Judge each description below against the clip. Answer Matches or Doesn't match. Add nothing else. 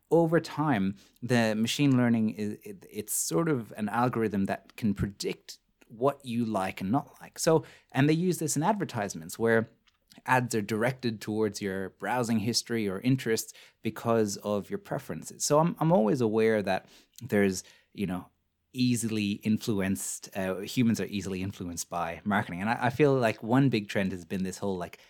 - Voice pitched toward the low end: Matches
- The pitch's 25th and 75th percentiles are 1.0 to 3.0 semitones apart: Doesn't match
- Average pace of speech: Matches